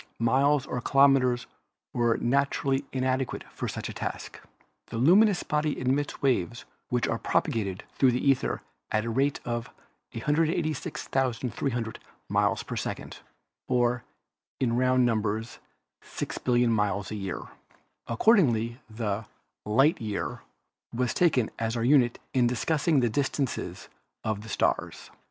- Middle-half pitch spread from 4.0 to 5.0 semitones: No, average, 3.2 semitones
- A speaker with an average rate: No, slow, 130 wpm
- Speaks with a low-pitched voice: Yes, low, 125 Hz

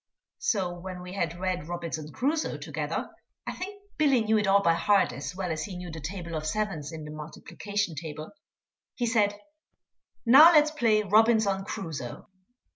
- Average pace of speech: Yes, average, 170 wpm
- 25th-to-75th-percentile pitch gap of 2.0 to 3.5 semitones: No, average, 5.1 semitones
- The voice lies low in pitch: No, high, 190 Hz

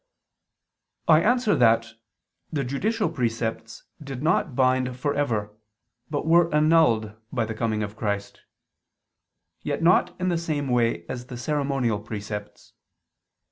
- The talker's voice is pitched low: Yes, low, 125 Hz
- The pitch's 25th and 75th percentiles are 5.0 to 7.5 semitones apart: Yes, wide, 5.6 semitones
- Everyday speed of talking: No, slow, 130 wpm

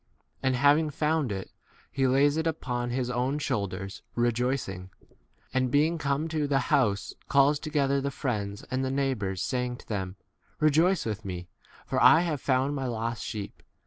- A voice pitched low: Yes, low, 130 Hz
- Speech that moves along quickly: No, average, 170 wpm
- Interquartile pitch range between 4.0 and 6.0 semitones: Yes, average, 4.4 semitones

